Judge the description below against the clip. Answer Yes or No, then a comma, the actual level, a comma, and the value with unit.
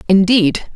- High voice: Yes, high, 195 Hz